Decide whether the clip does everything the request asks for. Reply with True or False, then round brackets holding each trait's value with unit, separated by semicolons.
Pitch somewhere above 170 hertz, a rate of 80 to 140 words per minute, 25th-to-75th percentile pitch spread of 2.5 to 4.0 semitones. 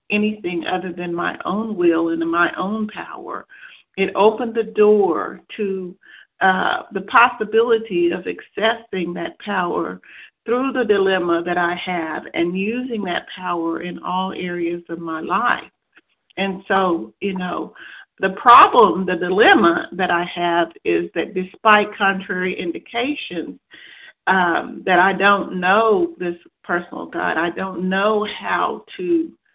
True (190 Hz; 135 wpm; 3.5 semitones)